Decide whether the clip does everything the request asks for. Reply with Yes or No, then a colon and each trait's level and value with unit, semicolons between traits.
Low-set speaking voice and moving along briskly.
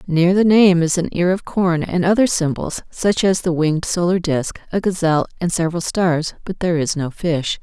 No: medium, 175 Hz; fast, 215 wpm